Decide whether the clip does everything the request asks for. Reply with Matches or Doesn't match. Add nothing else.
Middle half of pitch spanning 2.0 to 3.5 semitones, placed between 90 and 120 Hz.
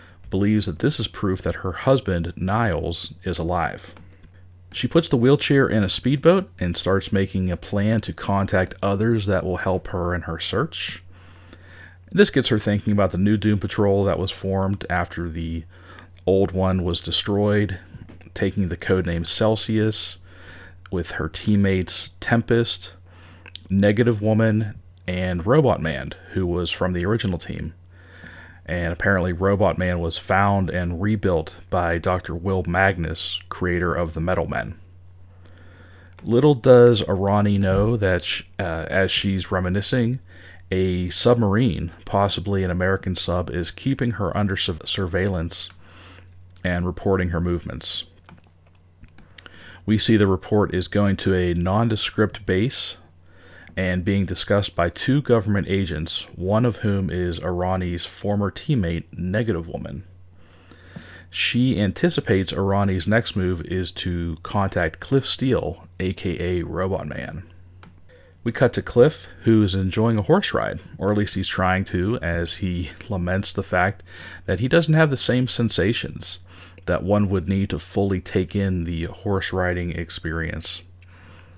Matches